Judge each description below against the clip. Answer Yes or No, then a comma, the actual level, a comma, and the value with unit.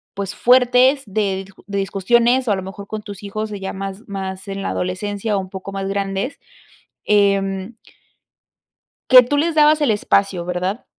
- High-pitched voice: Yes, high, 200 Hz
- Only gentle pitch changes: No, average, 3.1 semitones